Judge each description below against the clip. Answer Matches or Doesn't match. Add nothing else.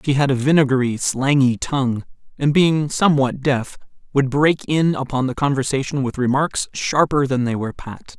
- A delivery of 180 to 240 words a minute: Doesn't match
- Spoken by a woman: Doesn't match